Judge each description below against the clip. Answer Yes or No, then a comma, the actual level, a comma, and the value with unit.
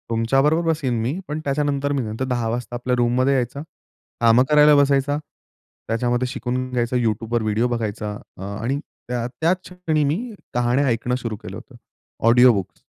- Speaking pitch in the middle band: No, low, 125 Hz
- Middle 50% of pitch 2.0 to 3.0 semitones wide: No, average, 3.4 semitones